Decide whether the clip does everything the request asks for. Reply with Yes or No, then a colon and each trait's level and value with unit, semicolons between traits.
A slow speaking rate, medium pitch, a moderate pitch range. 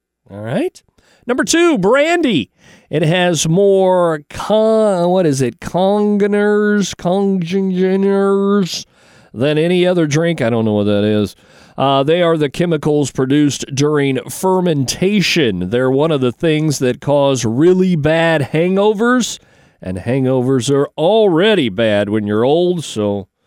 No: slow, 130 wpm; medium, 165 Hz; wide, 6.5 semitones